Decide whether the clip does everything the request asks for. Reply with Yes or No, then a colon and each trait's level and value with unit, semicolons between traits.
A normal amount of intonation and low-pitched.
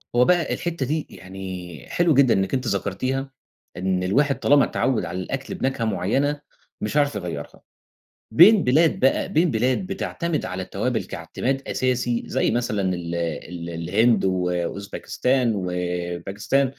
No: wide, 6.8 semitones; low, 115 Hz